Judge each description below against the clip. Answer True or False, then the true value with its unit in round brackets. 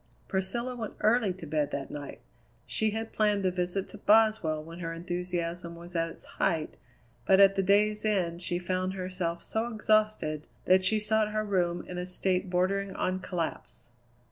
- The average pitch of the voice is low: False (185 Hz)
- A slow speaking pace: False (175 wpm)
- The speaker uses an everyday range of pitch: True (3.5 semitones)